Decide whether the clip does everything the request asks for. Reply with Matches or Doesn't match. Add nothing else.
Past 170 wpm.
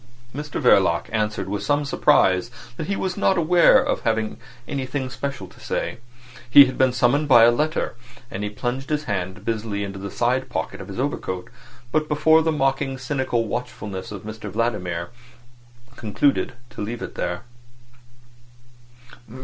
Doesn't match